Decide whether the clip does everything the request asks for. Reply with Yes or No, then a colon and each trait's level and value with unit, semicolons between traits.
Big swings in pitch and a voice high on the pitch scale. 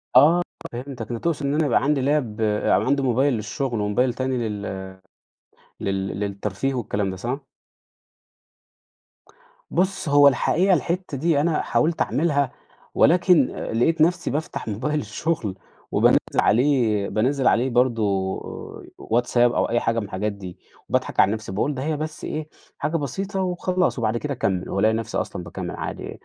No: wide, 6.0 semitones; low, 125 Hz